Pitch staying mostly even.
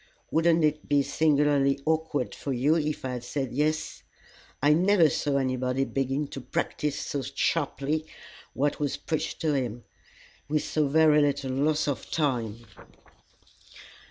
Yes: narrow, 2.3 semitones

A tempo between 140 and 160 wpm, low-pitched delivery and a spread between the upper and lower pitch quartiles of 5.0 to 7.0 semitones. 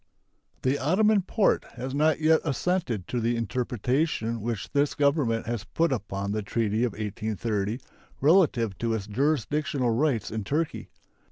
Yes: average, 145 wpm; low, 120 Hz; average, 5.3 semitones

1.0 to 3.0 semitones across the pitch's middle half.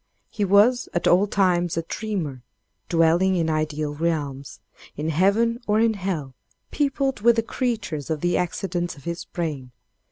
No: average, 5.0 semitones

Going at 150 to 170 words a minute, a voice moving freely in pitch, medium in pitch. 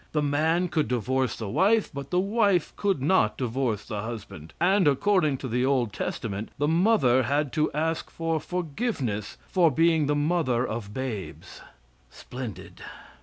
Yes: average, 155 wpm; wide, 5.7 semitones; medium, 145 Hz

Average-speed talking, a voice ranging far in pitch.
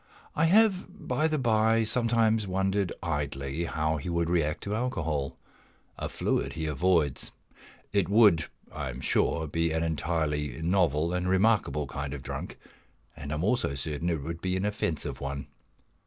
Yes: average, 160 wpm; wide, 5.7 semitones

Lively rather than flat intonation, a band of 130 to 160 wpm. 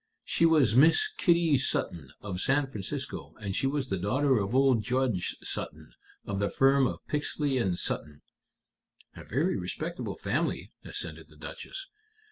Yes: wide, 6.5 semitones; average, 150 wpm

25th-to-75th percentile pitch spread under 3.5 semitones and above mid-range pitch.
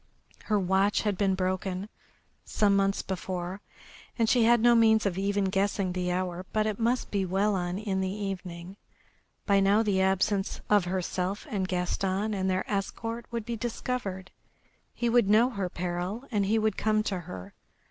Yes: narrow, 2.5 semitones; high, 195 Hz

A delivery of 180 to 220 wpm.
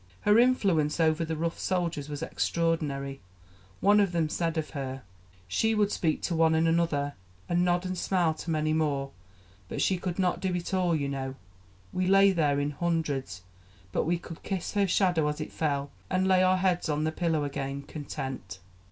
Yes: average, 195 wpm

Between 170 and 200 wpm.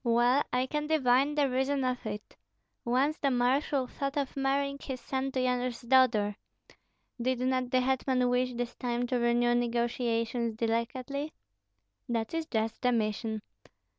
No: average, 150 wpm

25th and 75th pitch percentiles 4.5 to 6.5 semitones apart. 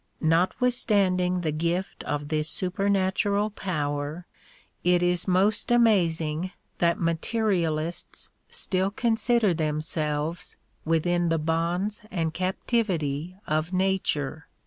No: average, 3.4 semitones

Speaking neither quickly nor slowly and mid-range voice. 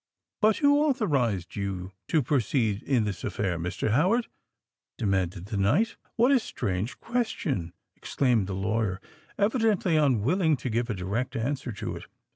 No: average, 145 wpm; low, 120 Hz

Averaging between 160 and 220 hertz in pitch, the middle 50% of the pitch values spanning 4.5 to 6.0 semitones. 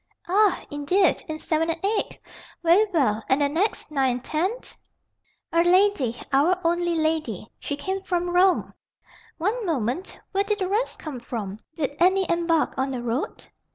No: very high, 330 Hz; average, 5.2 semitones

